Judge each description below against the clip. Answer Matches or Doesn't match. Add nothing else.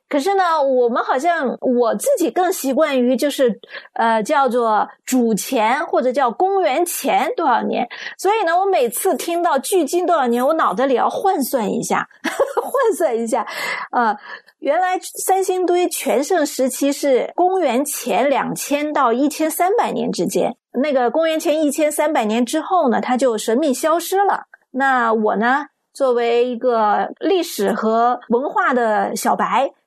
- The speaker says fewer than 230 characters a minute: Doesn't match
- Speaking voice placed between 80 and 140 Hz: Doesn't match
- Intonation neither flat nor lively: Doesn't match